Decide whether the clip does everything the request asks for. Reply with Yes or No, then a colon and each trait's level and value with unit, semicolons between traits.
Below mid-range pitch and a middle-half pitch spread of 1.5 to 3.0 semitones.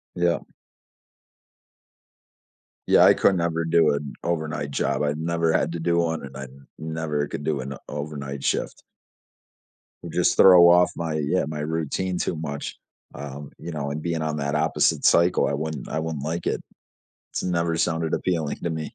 Yes: very low, 80 Hz; narrow, 2.4 semitones